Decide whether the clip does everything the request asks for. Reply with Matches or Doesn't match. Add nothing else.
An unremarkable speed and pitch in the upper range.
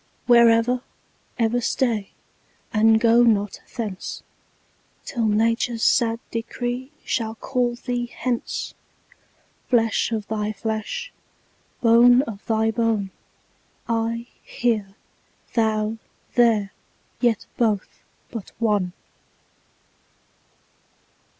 Doesn't match